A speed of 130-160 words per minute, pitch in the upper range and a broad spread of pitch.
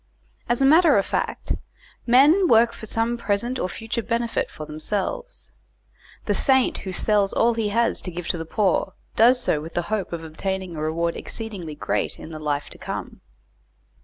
No: average, 185 wpm; high, 205 Hz; wide, 5.7 semitones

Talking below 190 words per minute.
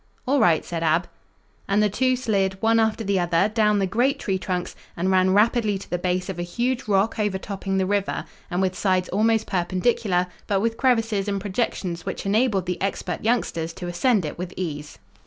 No: average, 195 wpm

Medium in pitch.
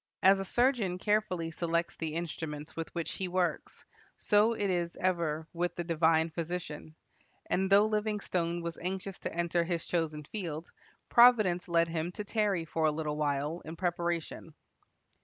Yes: medium, 170 Hz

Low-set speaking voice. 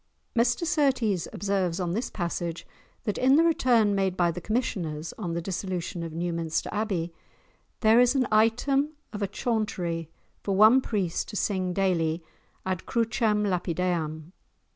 No: high, 195 Hz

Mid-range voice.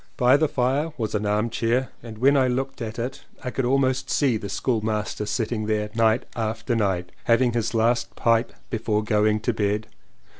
No: low, 115 Hz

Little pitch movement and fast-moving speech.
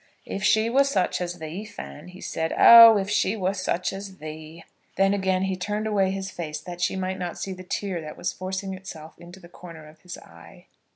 Yes: narrow, 2.2 semitones; fast, 220 wpm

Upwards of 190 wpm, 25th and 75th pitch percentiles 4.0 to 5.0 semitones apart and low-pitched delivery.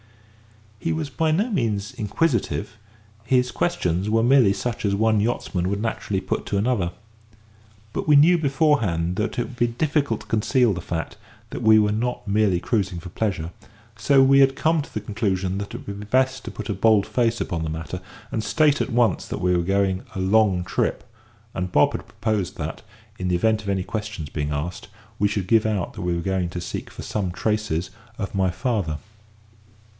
Yes: average, 200 wpm; average, 4.7 semitones; low, 105 Hz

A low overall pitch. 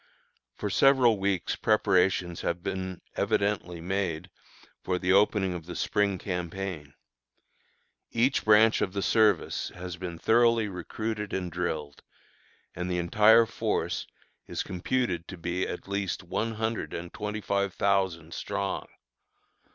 Yes: very low, 95 Hz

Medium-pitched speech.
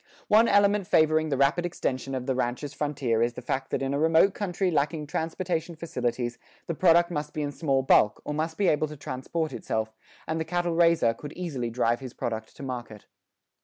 Yes: medium, 150 Hz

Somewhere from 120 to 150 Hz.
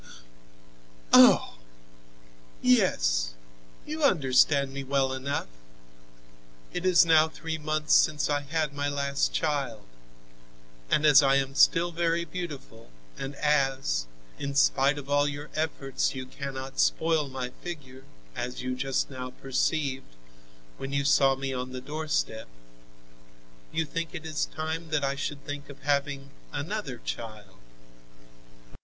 Yes: medium, 140 Hz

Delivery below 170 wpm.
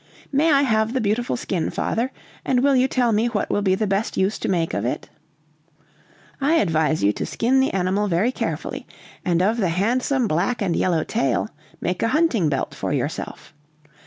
No: average, 190 wpm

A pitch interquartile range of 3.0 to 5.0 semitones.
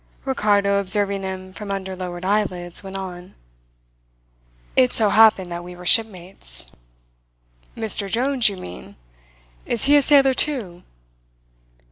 Yes: average, 3.5 semitones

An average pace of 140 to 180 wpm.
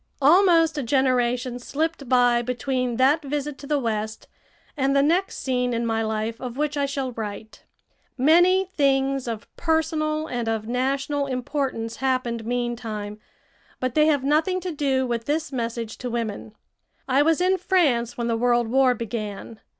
Yes: average, 160 wpm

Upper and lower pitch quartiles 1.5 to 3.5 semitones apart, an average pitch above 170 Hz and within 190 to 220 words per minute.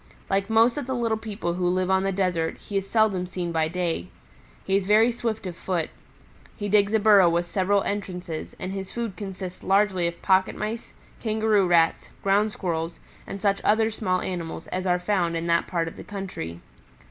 Yes: average, 3.1 semitones; high, 190 Hz; average, 195 wpm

